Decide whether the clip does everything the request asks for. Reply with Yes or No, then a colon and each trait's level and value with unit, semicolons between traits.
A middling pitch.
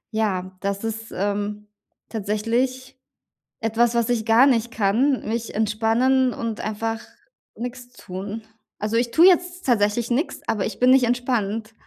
No: high, 225 Hz